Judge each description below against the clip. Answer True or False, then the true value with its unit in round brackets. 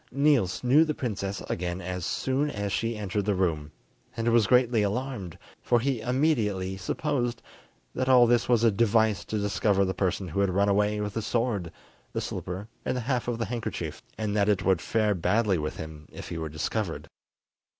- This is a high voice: False (105 Hz)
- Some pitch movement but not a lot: True (4.2 semitones)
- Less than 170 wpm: False (190 wpm)